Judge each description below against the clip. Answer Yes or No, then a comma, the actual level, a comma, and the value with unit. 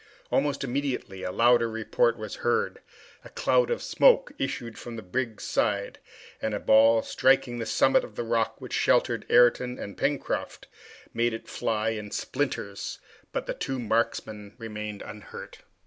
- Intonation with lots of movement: No, average, 3.4 semitones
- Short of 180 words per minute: Yes, average, 155 wpm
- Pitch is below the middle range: Yes, low, 115 Hz